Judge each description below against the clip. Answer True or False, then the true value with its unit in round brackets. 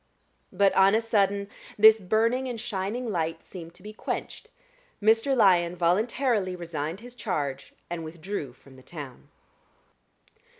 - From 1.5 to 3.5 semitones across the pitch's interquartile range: False (4.7 semitones)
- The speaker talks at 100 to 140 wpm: True (135 wpm)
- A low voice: False (195 Hz)